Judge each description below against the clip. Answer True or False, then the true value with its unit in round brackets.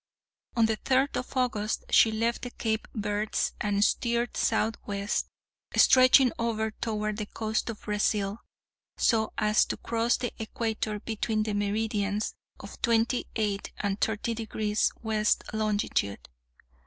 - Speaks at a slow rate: True (130 wpm)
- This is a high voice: True (220 Hz)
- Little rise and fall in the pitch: True (1.7 semitones)